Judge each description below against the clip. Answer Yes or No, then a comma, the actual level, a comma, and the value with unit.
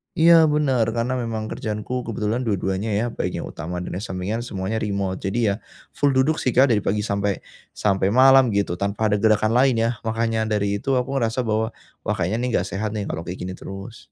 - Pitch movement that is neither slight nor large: Yes, average, 3.6 semitones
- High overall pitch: No, low, 110 Hz